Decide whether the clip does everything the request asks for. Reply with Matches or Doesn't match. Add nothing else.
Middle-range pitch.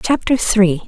Doesn't match